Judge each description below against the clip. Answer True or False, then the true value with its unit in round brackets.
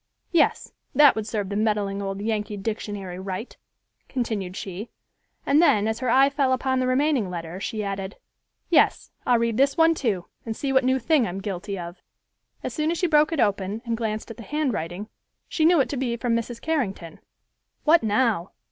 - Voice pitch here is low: False (225 Hz)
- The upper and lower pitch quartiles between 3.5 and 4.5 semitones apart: False (5.1 semitones)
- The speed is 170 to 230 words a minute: True (190 wpm)